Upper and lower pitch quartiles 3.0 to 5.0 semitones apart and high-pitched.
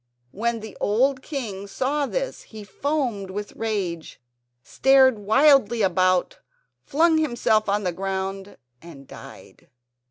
No: wide, 5.6 semitones; high, 215 Hz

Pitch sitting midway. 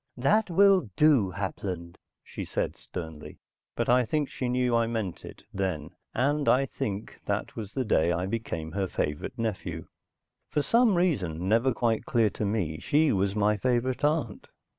No: low, 115 Hz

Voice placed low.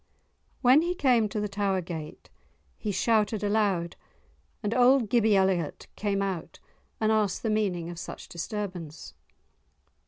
No: high, 205 Hz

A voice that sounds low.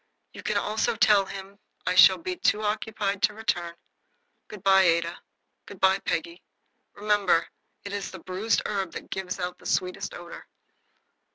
No: high, 195 Hz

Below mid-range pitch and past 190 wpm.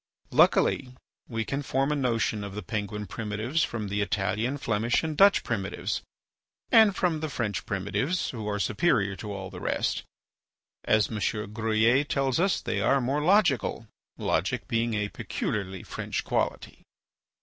No: low, 115 Hz; average, 150 wpm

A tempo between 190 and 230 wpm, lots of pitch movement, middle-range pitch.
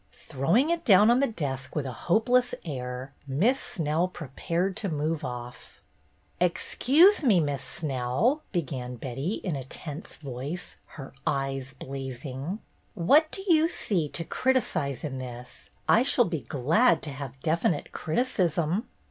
No: average, 145 wpm; wide, 7.8 semitones; medium, 155 Hz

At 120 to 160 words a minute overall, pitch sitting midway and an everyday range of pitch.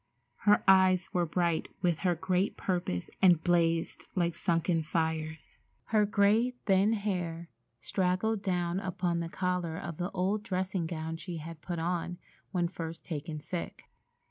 No: average, 145 wpm; medium, 175 Hz; narrow, 2.3 semitones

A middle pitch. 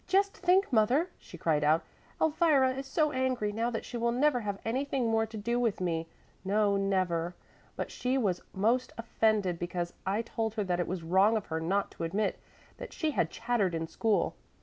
No: high, 215 Hz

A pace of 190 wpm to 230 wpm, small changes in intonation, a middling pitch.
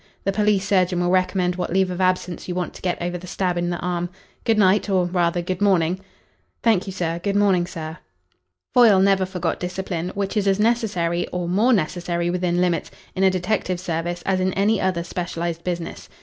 Yes: average, 200 wpm; narrow, 1.8 semitones; medium, 180 Hz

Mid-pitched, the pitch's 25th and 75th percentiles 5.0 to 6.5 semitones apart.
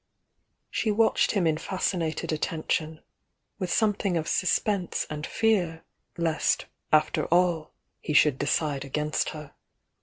No: medium, 160 Hz; average, 3.3 semitones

